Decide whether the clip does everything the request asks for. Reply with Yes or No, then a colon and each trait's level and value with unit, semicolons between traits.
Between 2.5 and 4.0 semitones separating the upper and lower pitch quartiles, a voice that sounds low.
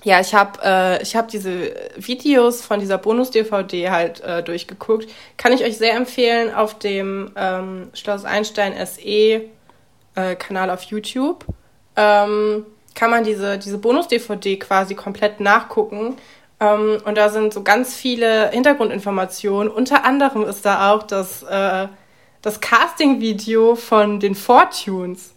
No: average, 2.8 semitones; high, 210 Hz